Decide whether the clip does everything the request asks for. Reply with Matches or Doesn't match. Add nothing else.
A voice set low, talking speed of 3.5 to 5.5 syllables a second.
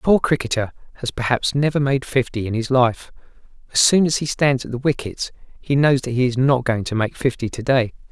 Doesn't match